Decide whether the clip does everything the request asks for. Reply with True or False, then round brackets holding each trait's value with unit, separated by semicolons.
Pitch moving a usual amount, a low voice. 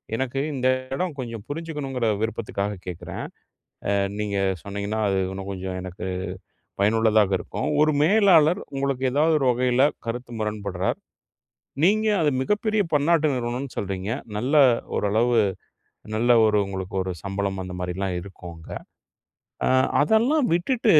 False (6.9 semitones; 115 Hz)